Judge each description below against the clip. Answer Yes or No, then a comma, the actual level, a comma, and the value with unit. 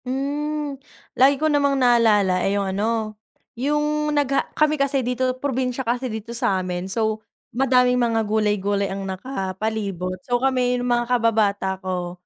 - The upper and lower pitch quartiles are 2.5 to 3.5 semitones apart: No, average, 4.6 semitones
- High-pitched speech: Yes, high, 240 Hz